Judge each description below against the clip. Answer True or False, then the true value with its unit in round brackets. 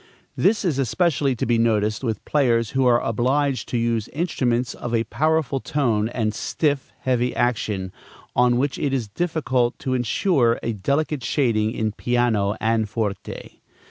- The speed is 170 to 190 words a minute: False (155 wpm)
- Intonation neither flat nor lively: True (3.6 semitones)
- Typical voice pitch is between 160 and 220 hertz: False (120 Hz)